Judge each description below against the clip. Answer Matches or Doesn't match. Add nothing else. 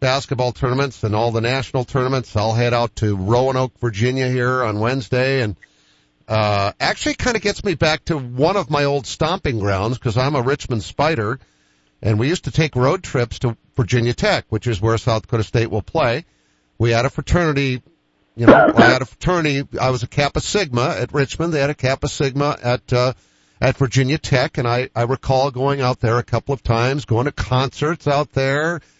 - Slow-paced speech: Doesn't match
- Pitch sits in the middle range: Doesn't match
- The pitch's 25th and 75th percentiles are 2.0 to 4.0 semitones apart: Matches